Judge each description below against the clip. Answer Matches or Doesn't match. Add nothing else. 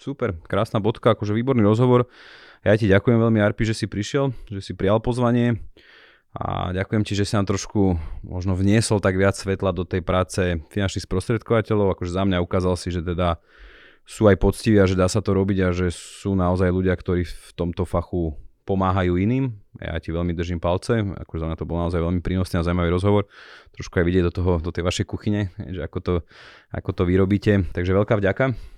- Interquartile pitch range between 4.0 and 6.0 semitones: Doesn't match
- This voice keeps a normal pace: Doesn't match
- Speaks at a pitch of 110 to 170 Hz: Doesn't match